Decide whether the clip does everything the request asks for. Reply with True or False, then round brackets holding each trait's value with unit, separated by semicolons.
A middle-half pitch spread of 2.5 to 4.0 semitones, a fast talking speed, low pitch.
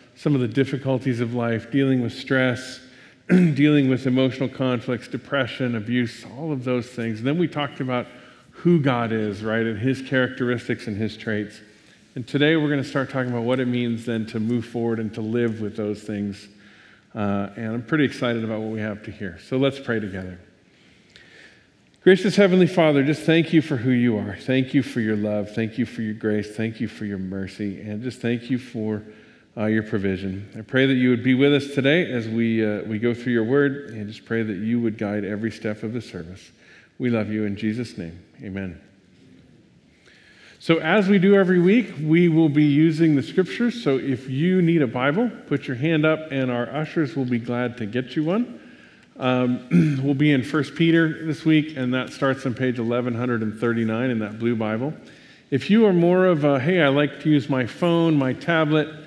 False (4.6 semitones; 210 wpm; 125 Hz)